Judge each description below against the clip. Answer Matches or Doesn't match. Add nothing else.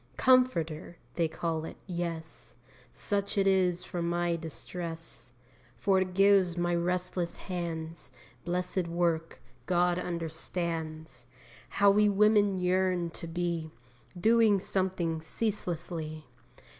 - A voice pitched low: Doesn't match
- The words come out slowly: Matches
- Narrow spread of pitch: Matches